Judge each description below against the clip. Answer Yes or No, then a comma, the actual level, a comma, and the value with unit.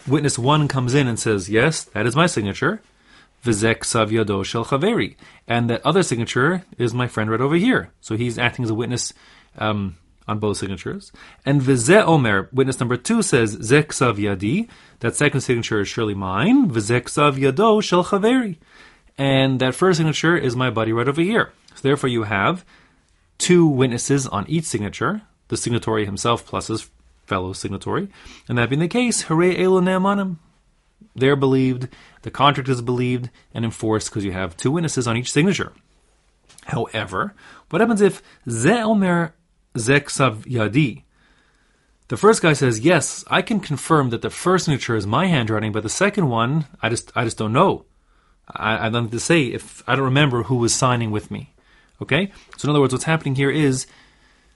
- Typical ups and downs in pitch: No, wide, 6.1 semitones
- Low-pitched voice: Yes, low, 130 Hz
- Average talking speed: Yes, average, 170 wpm